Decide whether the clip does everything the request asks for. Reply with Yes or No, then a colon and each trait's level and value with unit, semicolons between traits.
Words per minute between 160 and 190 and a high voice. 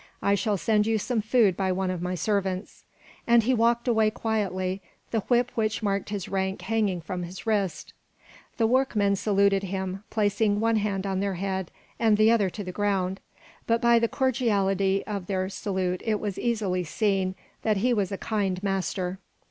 Yes: average, 180 wpm; high, 200 Hz